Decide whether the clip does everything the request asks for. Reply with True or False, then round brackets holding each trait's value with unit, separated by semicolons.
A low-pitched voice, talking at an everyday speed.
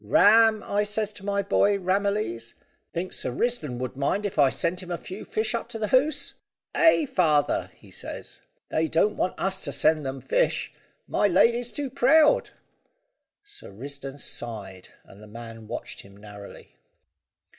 False (185 Hz; 165 wpm)